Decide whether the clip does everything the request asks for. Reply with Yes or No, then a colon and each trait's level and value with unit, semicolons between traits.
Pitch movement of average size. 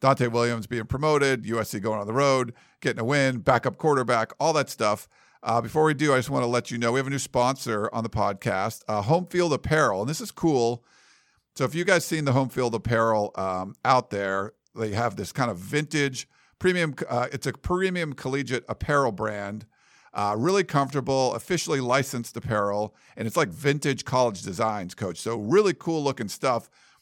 Yes: average, 3.9 semitones